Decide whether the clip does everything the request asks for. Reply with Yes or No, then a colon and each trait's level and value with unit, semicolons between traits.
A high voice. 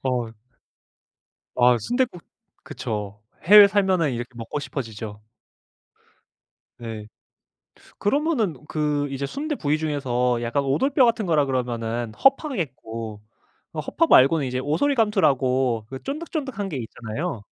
No: medium, 140 Hz